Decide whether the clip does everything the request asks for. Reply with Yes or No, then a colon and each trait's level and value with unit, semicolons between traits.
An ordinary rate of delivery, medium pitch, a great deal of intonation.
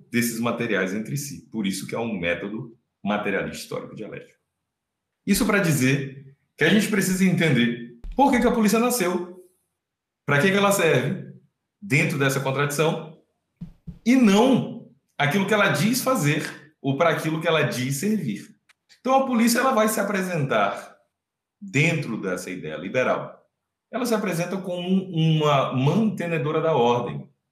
Yes: average, 150 wpm; medium, 160 Hz; wide, 7.0 semitones